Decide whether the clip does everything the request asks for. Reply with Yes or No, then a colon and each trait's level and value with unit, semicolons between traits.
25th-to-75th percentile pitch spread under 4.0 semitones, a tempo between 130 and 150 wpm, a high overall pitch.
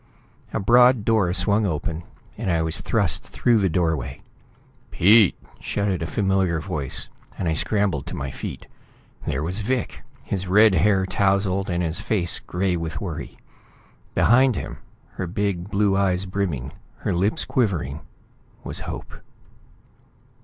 No: average, 3.4 semitones; average, 140 wpm; very low, 95 Hz